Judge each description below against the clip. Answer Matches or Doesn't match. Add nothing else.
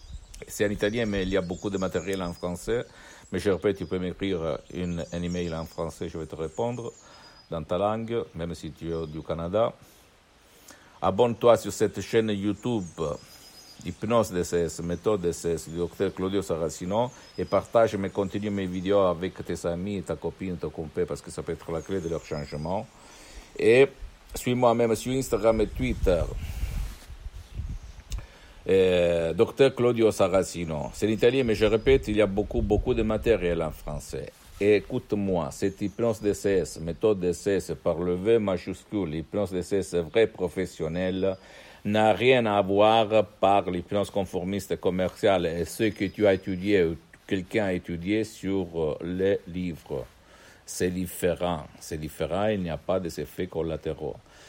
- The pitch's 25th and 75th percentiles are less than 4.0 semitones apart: Matches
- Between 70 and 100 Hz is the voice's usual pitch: Matches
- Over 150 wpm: Matches